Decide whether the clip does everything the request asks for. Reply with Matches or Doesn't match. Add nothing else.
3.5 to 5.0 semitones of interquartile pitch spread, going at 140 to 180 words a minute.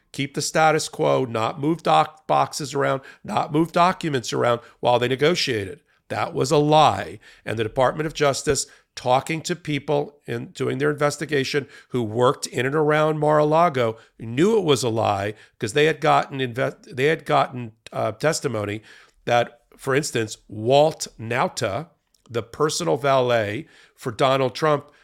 Matches